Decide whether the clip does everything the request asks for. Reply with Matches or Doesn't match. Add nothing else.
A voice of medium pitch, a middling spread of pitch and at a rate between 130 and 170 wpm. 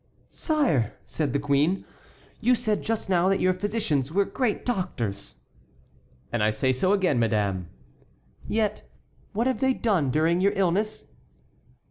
Doesn't match